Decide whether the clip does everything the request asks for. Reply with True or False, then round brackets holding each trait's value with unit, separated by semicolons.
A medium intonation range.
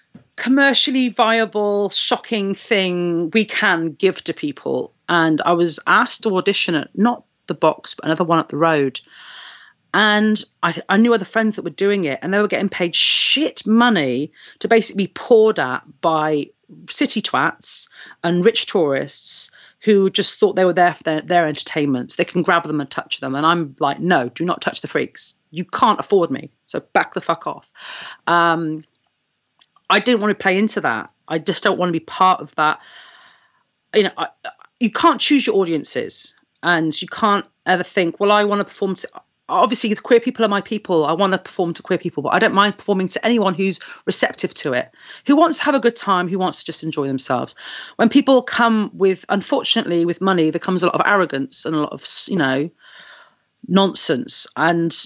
True (5.0 semitones)